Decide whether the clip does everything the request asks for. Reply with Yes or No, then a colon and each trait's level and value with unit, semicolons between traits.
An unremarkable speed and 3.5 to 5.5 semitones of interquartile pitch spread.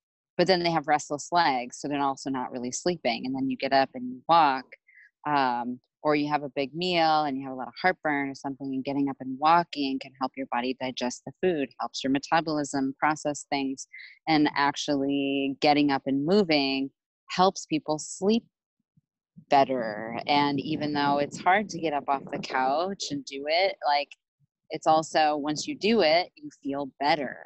No: average, 190 wpm; narrow, 2.6 semitones